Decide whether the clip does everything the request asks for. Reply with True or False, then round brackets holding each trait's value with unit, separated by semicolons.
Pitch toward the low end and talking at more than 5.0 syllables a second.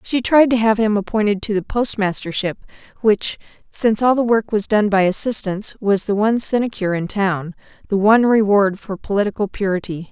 False (205 Hz; 5.5 syllables/s)